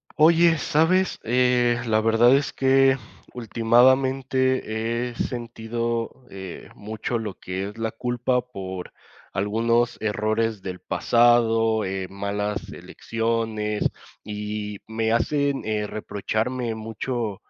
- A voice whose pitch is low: Yes, low, 115 Hz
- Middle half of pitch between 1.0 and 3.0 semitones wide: Yes, average, 2.7 semitones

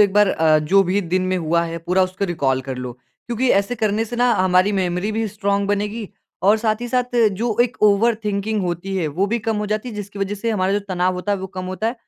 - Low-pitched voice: No, high, 200 Hz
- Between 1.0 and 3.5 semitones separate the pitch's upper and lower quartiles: Yes, average, 2.9 semitones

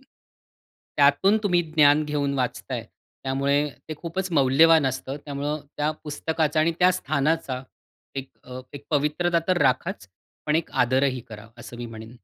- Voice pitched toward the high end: No, medium, 145 Hz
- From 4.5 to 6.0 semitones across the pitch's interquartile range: No, average, 3.2 semitones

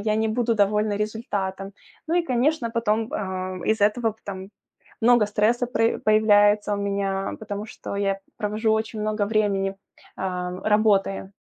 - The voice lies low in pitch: No, high, 210 Hz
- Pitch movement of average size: No, narrow, 1.9 semitones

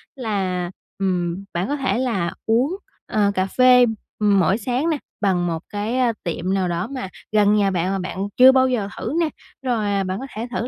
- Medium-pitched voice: No, high, 205 Hz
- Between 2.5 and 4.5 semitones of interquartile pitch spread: No, average, 5.1 semitones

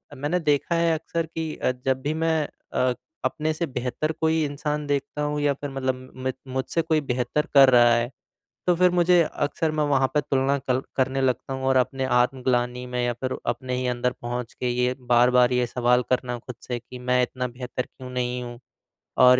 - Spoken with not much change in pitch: No, average, 3.0 semitones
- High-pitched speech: No, low, 130 Hz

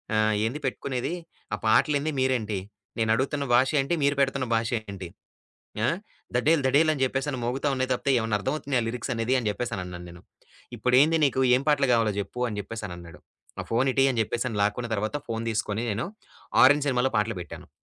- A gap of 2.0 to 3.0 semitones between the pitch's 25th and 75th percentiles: No, average, 3.7 semitones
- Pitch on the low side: Yes, low, 125 Hz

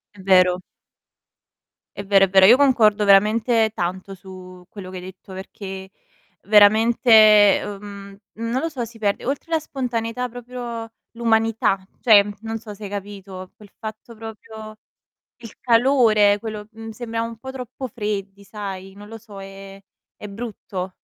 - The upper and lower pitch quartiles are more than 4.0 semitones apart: No, average, 2.7 semitones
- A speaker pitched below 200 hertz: No, high, 215 Hz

